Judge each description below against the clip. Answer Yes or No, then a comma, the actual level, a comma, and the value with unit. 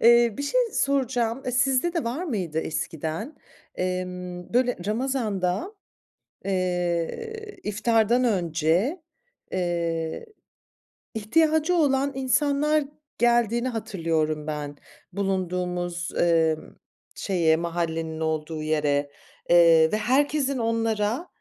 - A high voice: Yes, high, 200 Hz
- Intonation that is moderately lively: No, wide, 7.4 semitones